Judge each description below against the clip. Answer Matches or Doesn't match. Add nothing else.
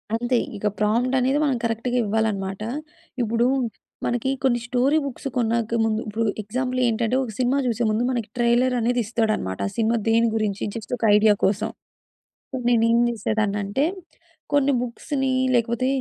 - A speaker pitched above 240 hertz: Doesn't match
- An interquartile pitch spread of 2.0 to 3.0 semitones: Matches